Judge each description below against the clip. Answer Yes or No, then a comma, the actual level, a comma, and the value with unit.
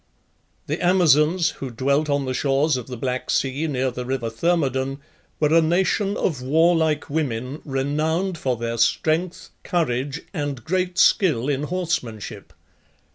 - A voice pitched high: No, medium, 145 Hz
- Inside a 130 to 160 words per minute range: Yes, average, 140 wpm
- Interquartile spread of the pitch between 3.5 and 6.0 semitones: Yes, average, 4.3 semitones